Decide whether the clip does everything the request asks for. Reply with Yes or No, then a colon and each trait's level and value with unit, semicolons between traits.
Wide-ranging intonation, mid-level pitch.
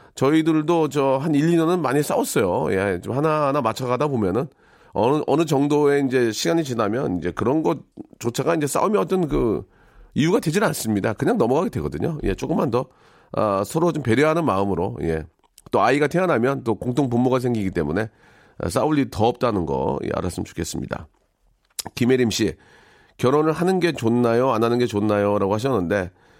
No: wide, 6.0 semitones; low, 125 Hz